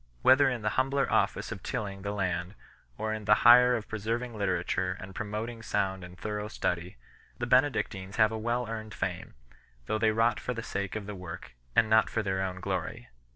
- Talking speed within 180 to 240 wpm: Yes, average, 200 wpm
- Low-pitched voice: Yes, low, 105 Hz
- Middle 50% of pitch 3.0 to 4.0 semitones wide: Yes, average, 3.3 semitones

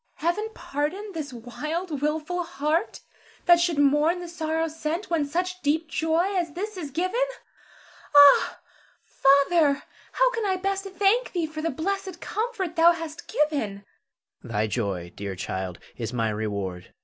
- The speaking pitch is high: Yes, very high, 320 Hz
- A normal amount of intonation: Yes, average, 4.4 semitones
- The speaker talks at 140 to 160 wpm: Yes, average, 155 wpm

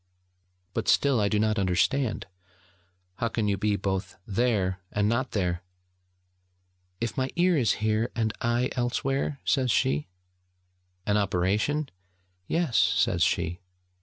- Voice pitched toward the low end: Yes, low, 110 Hz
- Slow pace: Yes, slow, 130 wpm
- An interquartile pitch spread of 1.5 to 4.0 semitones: No, average, 4.4 semitones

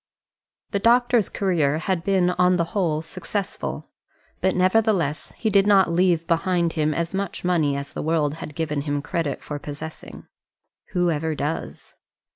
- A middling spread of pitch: Yes, average, 3.6 semitones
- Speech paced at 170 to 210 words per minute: No, average, 155 wpm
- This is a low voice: No, medium, 170 Hz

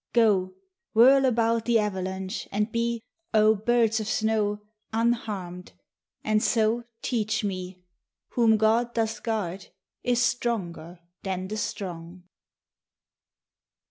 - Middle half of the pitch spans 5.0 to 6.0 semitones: No, average, 3.4 semitones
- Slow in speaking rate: Yes, slow, 110 wpm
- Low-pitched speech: No, high, 215 Hz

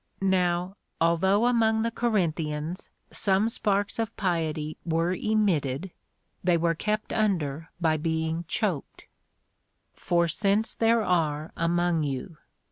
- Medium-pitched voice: Yes, medium, 175 Hz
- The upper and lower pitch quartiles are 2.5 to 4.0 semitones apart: No, average, 4.4 semitones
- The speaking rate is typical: No, slow, 115 wpm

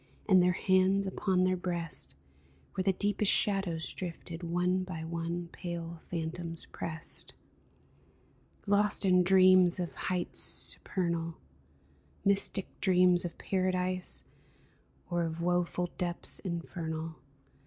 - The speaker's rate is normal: No, slow, 110 wpm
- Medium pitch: Yes, medium, 180 Hz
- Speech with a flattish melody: Yes, narrow, 1.7 semitones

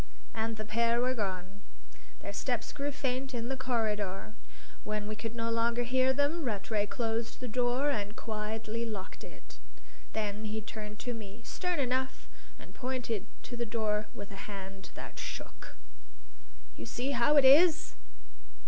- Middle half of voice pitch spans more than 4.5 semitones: No, average, 3.3 semitones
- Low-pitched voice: No, high, 230 Hz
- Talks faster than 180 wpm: No, average, 155 wpm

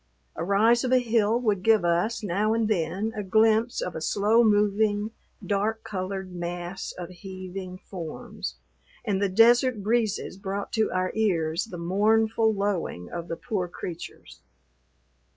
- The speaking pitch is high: Yes, high, 200 Hz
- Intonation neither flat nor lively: Yes, average, 3.3 semitones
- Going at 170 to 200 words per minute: No, average, 150 wpm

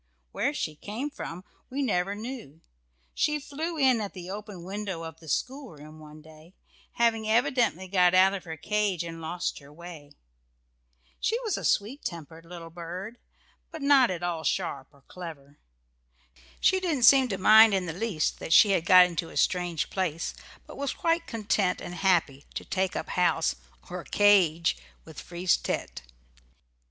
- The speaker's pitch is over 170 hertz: Yes, medium, 185 Hz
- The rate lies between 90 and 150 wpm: No, average, 165 wpm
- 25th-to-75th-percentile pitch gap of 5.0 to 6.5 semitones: Yes, wide, 5.4 semitones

